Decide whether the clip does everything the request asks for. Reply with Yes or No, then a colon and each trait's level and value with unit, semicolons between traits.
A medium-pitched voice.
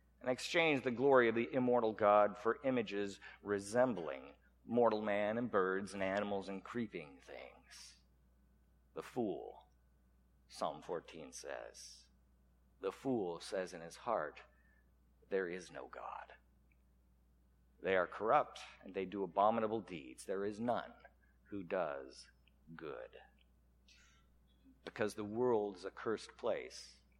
No: very low, 95 Hz